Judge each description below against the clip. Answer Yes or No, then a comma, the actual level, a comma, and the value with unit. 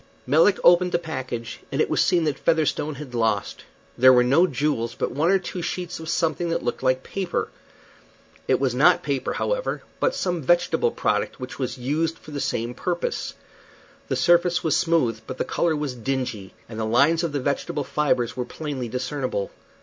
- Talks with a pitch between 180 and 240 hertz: No, medium, 145 Hz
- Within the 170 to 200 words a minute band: Yes, average, 190 wpm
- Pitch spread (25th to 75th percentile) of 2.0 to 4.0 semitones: No, average, 5.2 semitones